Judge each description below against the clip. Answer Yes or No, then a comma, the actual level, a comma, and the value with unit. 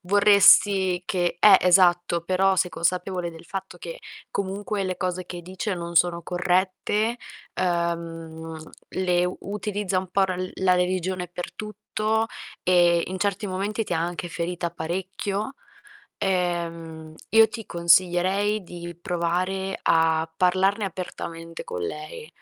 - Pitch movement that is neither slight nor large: No, narrow, 2.0 semitones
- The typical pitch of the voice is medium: Yes, medium, 180 Hz